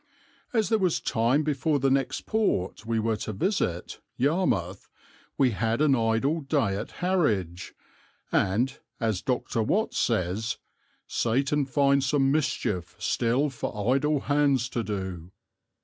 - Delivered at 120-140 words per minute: Yes, slow, 135 wpm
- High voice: No, low, 125 Hz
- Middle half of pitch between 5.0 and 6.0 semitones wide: Yes, average, 5.3 semitones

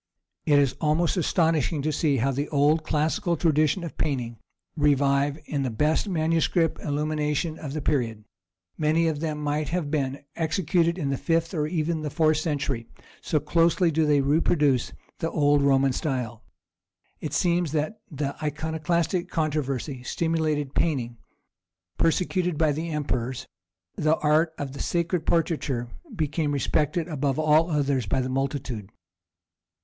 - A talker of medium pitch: Yes, medium, 150 Hz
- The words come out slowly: No, average, 145 wpm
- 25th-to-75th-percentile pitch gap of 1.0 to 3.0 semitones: Yes, average, 2.7 semitones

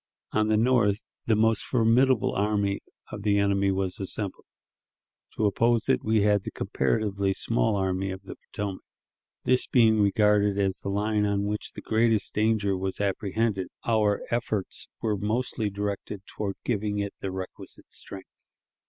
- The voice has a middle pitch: No, low, 105 Hz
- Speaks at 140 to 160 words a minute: Yes, average, 155 wpm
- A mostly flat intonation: Yes, narrow, 1.9 semitones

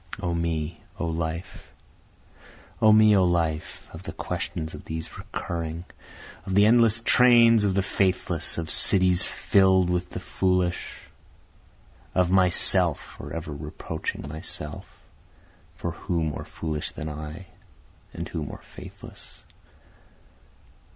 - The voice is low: Yes, very low, 85 Hz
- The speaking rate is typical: No, slow, 120 wpm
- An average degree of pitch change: Yes, average, 3.1 semitones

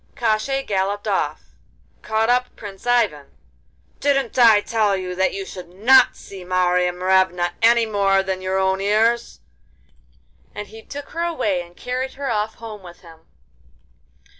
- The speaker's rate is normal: Yes, average, 150 wpm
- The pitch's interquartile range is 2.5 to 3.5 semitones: No, average, 3.9 semitones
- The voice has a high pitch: Yes, high, 205 Hz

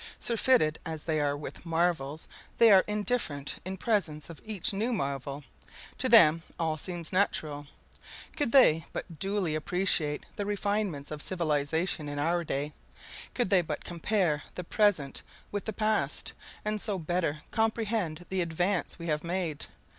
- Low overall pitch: No, medium, 175 Hz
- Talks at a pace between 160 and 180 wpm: No, average, 150 wpm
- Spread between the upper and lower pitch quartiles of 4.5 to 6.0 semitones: Yes, average, 5.0 semitones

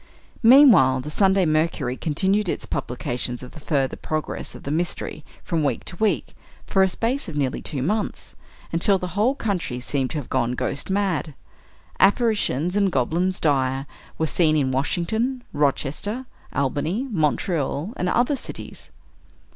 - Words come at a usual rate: Yes, average, 150 wpm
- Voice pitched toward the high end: No, medium, 165 Hz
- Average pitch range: No, wide, 6.3 semitones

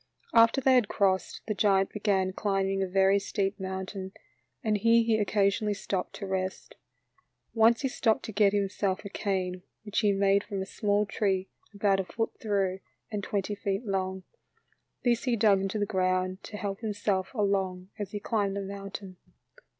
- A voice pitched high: Yes, high, 200 Hz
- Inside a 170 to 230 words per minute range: Yes, average, 175 wpm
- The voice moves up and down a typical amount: No, narrow, 1.6 semitones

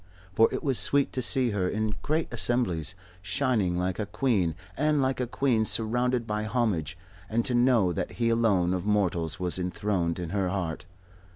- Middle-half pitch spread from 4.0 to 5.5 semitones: Yes, average, 5.1 semitones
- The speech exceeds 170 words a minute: Yes, average, 180 wpm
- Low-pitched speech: Yes, low, 105 Hz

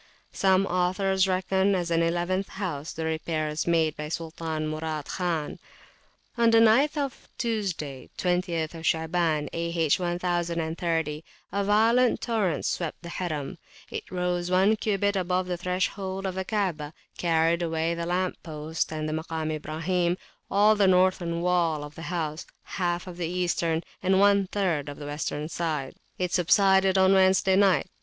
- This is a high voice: No, medium, 175 Hz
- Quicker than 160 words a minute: No, average, 155 wpm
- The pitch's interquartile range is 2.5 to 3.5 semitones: Yes, average, 2.8 semitones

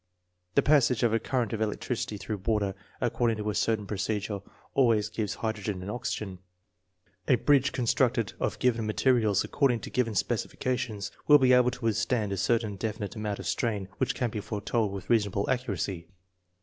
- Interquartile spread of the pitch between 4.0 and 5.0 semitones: No, average, 3.2 semitones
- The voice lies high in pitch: No, low, 110 Hz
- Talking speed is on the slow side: No, average, 175 wpm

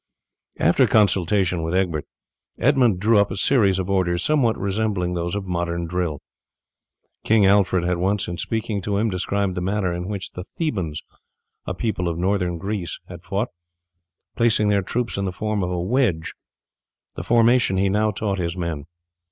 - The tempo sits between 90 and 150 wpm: No, average, 170 wpm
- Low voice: Yes, very low, 95 Hz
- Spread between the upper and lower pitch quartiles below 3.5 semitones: Yes, average, 3.1 semitones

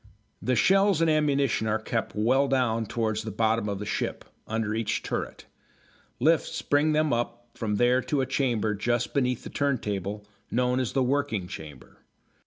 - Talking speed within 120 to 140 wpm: No, average, 170 wpm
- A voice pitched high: No, low, 120 Hz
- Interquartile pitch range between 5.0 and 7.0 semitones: No, average, 4.0 semitones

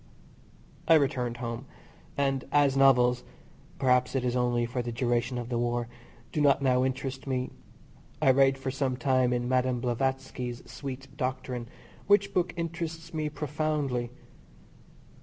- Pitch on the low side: Yes, low, 130 Hz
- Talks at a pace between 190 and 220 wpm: No, average, 140 wpm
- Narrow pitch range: Yes, narrow, 2.2 semitones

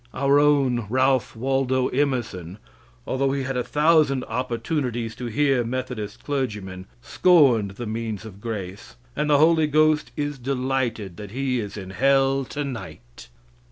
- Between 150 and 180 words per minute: No, average, 140 wpm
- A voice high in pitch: No, low, 130 Hz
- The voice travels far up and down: No, average, 3.8 semitones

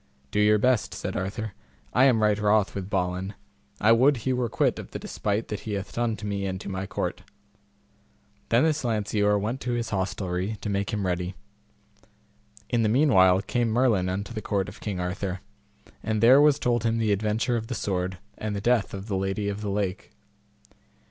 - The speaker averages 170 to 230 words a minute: Yes, average, 200 wpm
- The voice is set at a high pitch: No, low, 105 Hz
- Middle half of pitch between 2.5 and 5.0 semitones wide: Yes, average, 2.9 semitones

